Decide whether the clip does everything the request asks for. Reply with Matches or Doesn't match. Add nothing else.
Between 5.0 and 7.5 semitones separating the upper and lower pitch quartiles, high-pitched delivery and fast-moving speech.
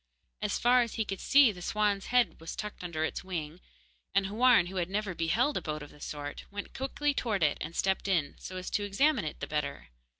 Matches